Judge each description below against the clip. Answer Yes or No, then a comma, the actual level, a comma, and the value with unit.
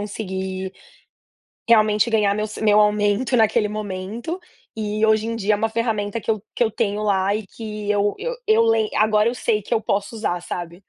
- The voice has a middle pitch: No, high, 210 Hz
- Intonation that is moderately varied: No, narrow, 1.5 semitones